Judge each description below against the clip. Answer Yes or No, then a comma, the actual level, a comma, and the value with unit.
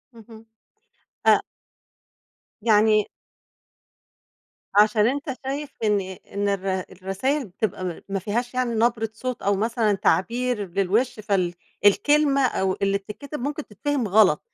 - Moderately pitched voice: No, high, 215 Hz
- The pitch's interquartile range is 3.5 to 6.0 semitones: Yes, average, 4.2 semitones